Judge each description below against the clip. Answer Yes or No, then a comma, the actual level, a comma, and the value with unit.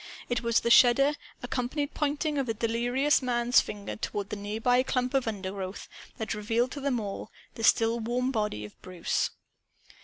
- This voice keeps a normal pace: Yes, average, 160 wpm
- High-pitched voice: Yes, high, 235 Hz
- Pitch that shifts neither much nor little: Yes, average, 3.1 semitones